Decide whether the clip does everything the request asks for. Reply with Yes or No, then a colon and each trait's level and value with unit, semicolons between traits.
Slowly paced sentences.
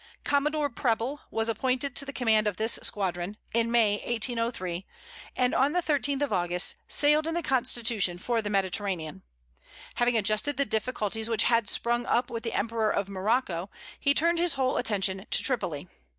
No: average, 170 wpm